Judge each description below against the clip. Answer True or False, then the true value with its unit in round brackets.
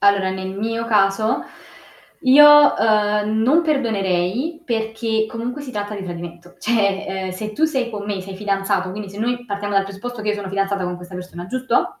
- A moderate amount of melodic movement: True (3.2 semitones)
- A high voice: True (210 Hz)